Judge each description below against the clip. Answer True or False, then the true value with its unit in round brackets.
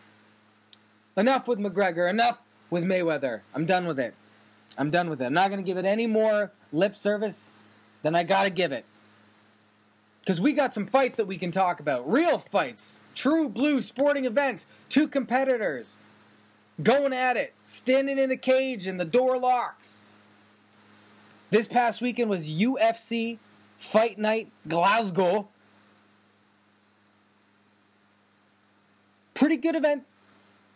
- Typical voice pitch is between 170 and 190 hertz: True (185 Hz)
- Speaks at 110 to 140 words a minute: True (135 wpm)